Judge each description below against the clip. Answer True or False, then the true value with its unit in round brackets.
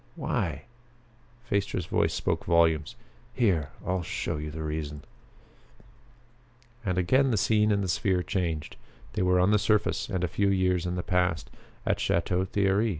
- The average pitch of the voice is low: True (90 Hz)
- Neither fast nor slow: True (155 wpm)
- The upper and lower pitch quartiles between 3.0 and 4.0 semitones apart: True (3.3 semitones)